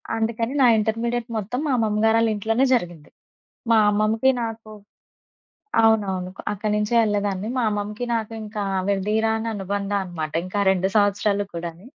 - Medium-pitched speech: No, high, 210 Hz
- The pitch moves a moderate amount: No, narrow, 2.0 semitones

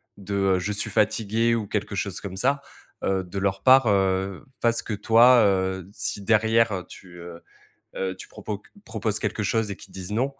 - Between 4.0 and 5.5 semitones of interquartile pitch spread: No, average, 2.8 semitones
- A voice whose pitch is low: Yes, low, 100 Hz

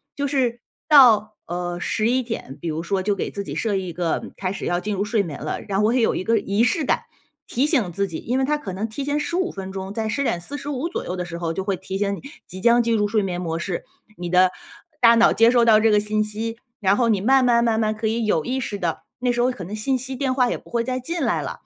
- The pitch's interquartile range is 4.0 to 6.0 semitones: Yes, average, 4.5 semitones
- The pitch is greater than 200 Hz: Yes, high, 215 Hz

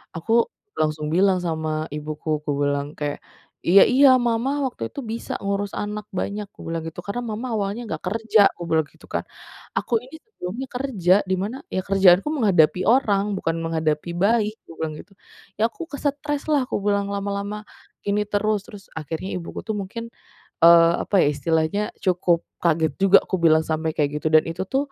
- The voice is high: Yes, high, 195 Hz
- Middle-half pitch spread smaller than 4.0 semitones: No, wide, 5.5 semitones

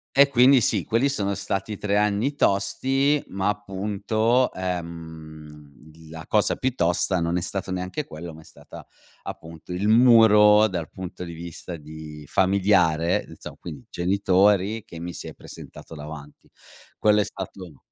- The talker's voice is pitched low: Yes, very low, 95 Hz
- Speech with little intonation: No, average, 4.2 semitones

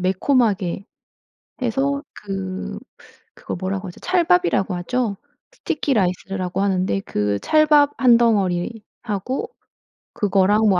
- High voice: Yes, high, 200 Hz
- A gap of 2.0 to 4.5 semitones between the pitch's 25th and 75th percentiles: No, average, 5.2 semitones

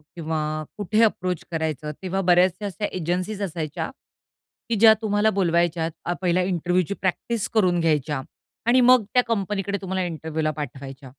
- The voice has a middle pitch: Yes, medium, 180 Hz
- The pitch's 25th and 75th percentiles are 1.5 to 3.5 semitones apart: No, average, 4.0 semitones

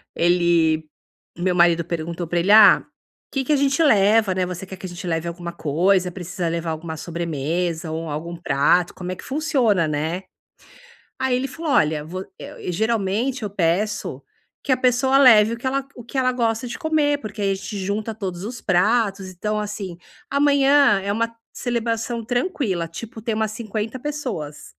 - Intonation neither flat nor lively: No, wide, 5.7 semitones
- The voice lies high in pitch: Yes, high, 200 Hz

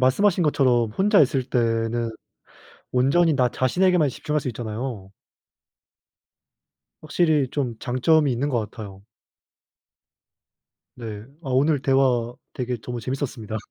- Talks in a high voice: No, low, 130 Hz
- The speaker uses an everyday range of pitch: Yes, average, 3.7 semitones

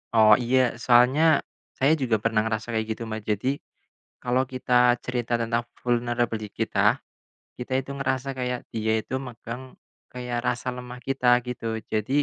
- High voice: No, low, 125 Hz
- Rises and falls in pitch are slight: Yes, narrow, 1.8 semitones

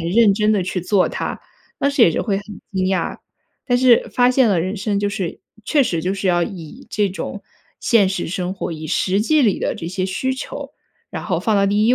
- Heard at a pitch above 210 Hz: No, high, 200 Hz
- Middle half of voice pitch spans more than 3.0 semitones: Yes, average, 3.5 semitones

